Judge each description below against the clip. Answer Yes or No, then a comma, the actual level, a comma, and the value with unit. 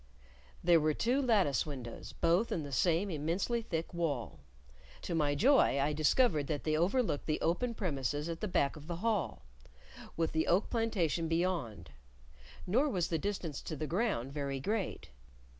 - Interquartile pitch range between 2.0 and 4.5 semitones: No, average, 5.3 semitones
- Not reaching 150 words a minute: No, average, 165 wpm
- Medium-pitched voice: Yes, medium, 165 Hz